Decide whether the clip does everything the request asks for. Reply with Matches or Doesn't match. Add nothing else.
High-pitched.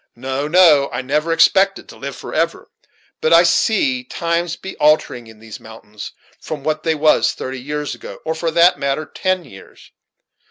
Doesn't match